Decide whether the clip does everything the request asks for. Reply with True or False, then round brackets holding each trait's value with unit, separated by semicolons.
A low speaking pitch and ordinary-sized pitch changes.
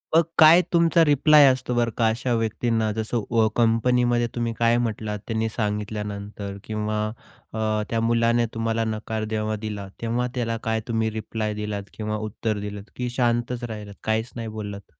False (115 Hz; 1.9 semitones)